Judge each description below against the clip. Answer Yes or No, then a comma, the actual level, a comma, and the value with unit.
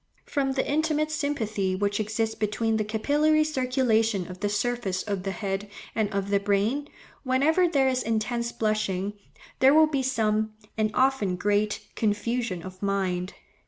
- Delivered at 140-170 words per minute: Yes, average, 155 wpm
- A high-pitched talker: Yes, high, 220 Hz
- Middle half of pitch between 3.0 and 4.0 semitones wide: No, average, 4.6 semitones